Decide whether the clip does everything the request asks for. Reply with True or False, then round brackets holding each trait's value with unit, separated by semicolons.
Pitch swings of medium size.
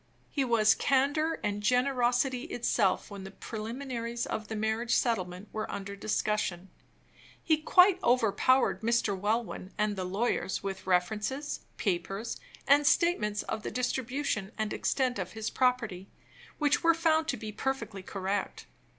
True (4.4 semitones)